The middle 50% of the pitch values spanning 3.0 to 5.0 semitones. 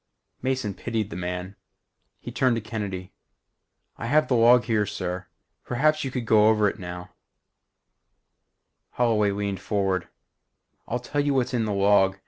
Yes: average, 4.1 semitones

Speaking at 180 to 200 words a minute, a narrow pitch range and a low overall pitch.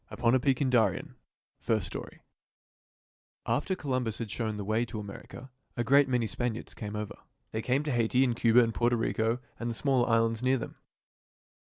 Yes: average, 185 wpm; narrow, 2.3 semitones; low, 120 Hz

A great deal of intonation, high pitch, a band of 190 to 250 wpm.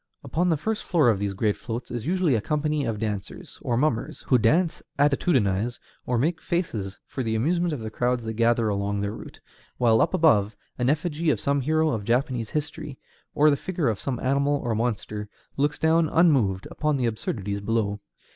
No: wide, 5.7 semitones; low, 125 Hz; average, 195 wpm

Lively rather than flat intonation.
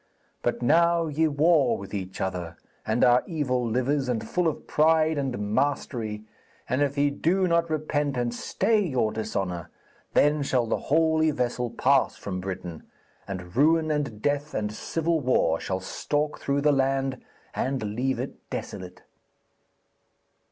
Yes: wide, 5.7 semitones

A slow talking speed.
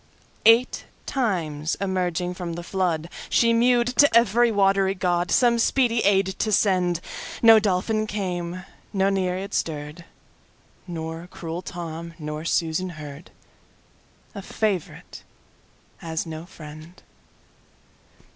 Yes: slow, 95 wpm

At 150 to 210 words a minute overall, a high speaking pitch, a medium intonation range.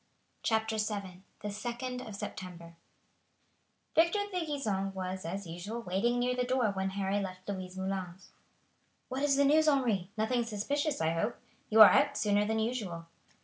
Yes: average, 160 wpm; high, 210 Hz; average, 4.7 semitones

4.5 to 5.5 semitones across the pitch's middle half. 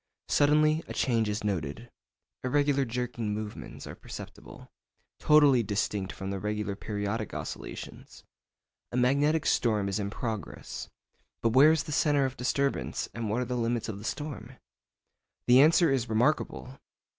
Yes: average, 4.8 semitones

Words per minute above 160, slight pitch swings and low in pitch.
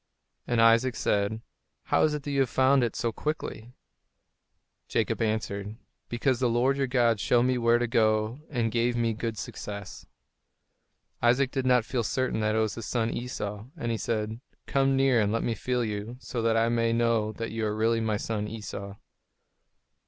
Yes: average, 185 wpm; narrow, 2.3 semitones; low, 115 Hz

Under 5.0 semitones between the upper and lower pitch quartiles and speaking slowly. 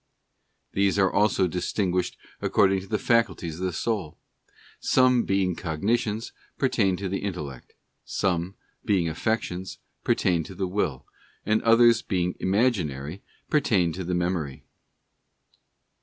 Yes: average, 3.4 semitones; slow, 125 wpm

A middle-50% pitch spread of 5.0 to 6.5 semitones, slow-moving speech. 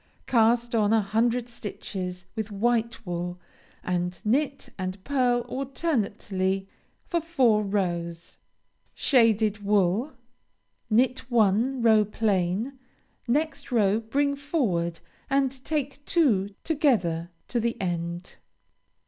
Yes: average, 5.3 semitones; slow, 105 wpm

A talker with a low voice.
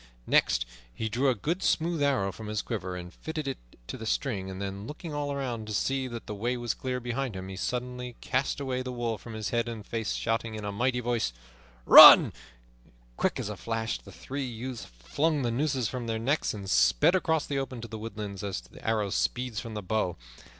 Yes: low, 115 Hz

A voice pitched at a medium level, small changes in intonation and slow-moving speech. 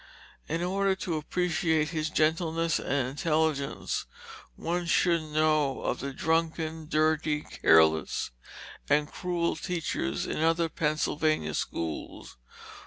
Yes: medium, 155 Hz; narrow, 1.9 semitones; slow, 105 wpm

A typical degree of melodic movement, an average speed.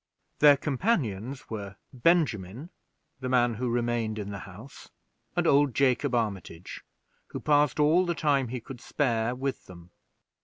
Yes: average, 4.9 semitones; average, 145 wpm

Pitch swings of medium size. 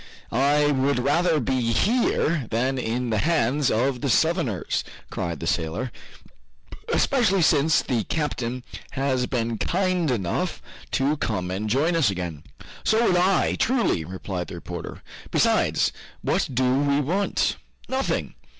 No: wide, 6.2 semitones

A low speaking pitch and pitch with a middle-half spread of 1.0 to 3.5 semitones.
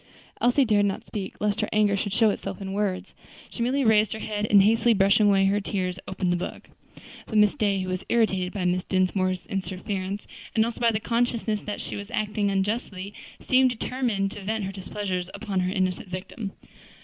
No: high, 205 Hz; narrow, 2.4 semitones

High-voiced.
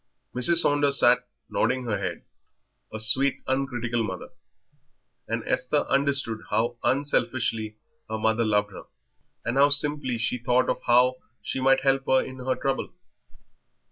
No: low, 125 Hz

